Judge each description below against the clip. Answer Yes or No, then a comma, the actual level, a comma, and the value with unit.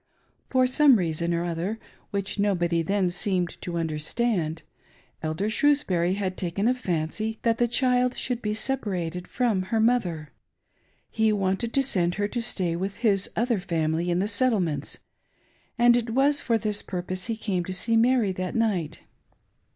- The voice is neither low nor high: No, high, 200 Hz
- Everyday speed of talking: Yes, average, 165 wpm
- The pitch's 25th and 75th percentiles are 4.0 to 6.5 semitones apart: Yes, average, 4.9 semitones